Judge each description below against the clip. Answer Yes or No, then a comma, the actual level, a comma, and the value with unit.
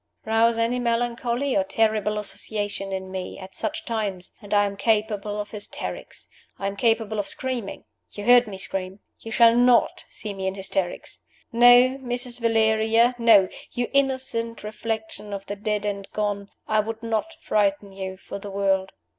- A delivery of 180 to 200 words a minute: No, average, 165 wpm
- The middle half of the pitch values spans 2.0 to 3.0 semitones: Yes, average, 2.7 semitones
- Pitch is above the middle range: Yes, high, 215 Hz